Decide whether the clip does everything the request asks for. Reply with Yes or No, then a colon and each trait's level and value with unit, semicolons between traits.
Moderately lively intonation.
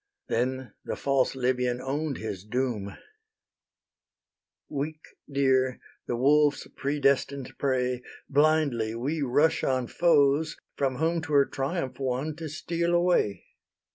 Yes: average, 3.2 semitones